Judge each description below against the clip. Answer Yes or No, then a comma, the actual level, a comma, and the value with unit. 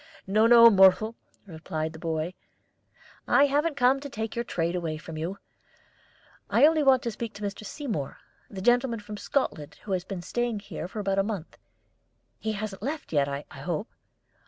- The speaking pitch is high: Yes, high, 205 Hz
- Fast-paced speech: No, average, 180 wpm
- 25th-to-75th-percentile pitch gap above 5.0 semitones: Yes, wide, 5.6 semitones